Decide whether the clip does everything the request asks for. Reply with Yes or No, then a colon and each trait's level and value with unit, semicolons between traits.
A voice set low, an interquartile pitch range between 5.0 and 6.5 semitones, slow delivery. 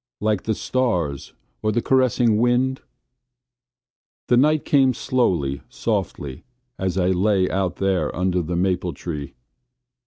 Yes: very low, 95 Hz; wide, 5.5 semitones; slow, 125 wpm